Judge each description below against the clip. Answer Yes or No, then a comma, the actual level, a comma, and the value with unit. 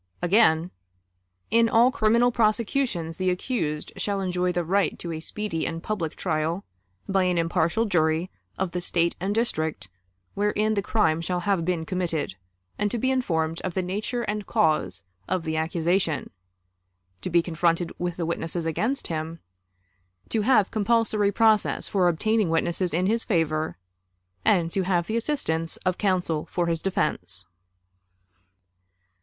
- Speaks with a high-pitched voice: No, medium, 180 Hz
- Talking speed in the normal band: Yes, average, 150 wpm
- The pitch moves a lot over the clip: No, average, 4.2 semitones